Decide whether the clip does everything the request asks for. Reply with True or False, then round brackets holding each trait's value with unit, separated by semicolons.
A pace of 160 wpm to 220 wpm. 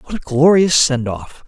True (205 wpm)